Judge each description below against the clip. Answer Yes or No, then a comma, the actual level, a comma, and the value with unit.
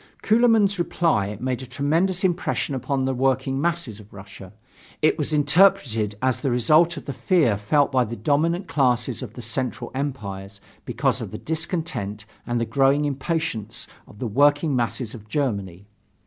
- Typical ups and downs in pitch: No, wide, 6.0 semitones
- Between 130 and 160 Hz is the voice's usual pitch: Yes, low, 135 Hz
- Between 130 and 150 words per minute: No, average, 160 wpm